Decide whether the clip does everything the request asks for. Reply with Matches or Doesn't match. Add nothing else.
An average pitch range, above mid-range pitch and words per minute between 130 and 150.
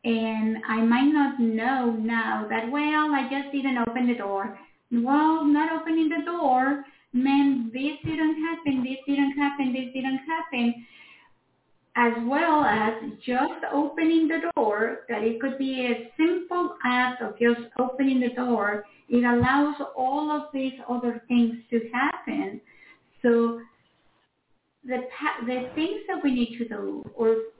Matches